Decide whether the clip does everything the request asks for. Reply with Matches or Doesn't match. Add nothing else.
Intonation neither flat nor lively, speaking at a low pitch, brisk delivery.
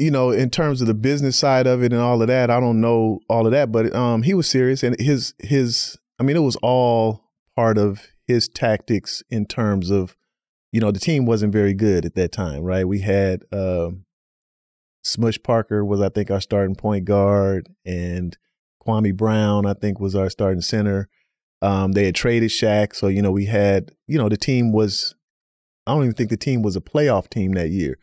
Matches